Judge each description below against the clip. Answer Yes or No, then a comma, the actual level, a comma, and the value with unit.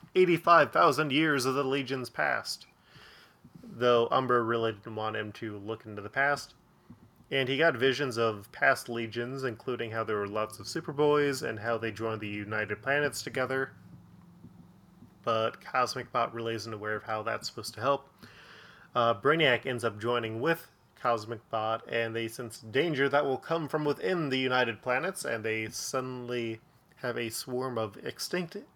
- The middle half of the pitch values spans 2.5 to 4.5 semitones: Yes, average, 3.5 semitones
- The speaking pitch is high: No, low, 120 Hz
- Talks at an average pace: Yes, average, 165 wpm